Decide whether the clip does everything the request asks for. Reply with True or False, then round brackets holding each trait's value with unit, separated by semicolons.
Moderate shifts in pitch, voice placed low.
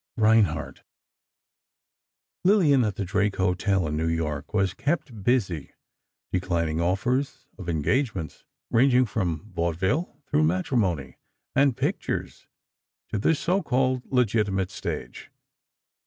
False (6.9 semitones; 100 Hz)